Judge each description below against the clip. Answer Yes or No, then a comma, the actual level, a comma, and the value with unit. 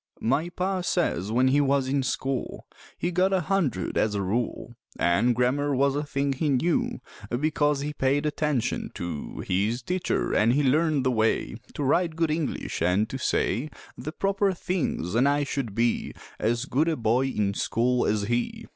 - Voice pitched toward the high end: No, low, 135 Hz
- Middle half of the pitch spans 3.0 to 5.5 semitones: Yes, average, 4.7 semitones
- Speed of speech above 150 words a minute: Yes, average, 180 wpm